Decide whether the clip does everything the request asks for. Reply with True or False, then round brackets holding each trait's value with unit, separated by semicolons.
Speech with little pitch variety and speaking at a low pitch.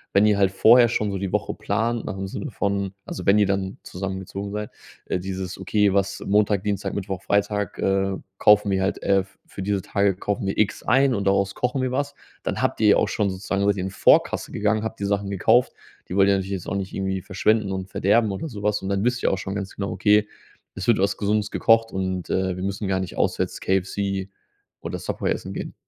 True (1.6 semitones; 100 Hz)